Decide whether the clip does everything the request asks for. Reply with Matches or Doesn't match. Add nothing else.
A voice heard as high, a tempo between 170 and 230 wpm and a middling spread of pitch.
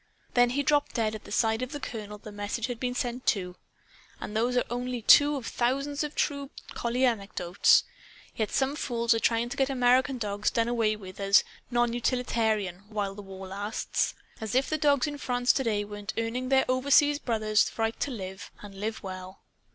Matches